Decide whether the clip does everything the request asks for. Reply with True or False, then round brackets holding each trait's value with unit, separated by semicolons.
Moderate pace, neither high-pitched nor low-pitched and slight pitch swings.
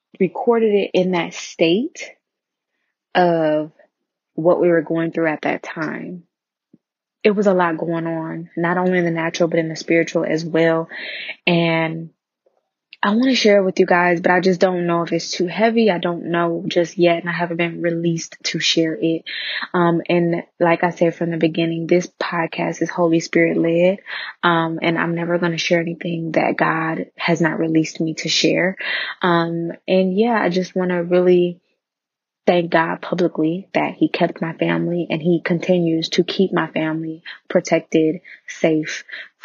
True (180 wpm; 170 Hz; 1.5 semitones)